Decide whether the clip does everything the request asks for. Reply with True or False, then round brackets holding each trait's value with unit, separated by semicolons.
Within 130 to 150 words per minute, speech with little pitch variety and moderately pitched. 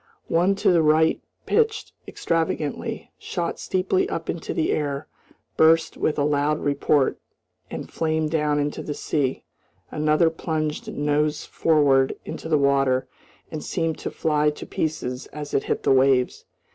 True (145 wpm; 2.0 semitones; 150 Hz)